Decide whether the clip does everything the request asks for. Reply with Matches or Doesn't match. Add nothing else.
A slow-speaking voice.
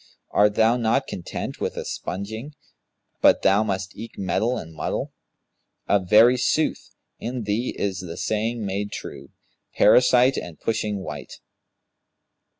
Matches